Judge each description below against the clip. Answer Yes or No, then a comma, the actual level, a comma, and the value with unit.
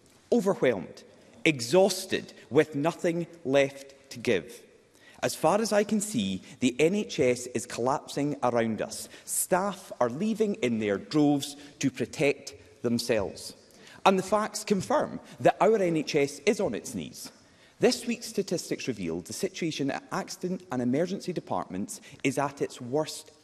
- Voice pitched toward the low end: No, medium, 155 Hz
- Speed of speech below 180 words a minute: Yes, average, 140 wpm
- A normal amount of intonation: No, wide, 6.0 semitones